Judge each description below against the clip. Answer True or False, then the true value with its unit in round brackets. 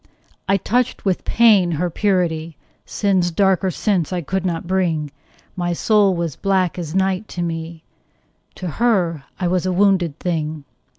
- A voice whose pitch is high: False (180 Hz)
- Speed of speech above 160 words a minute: False (155 wpm)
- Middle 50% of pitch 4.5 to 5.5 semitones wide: False (2.6 semitones)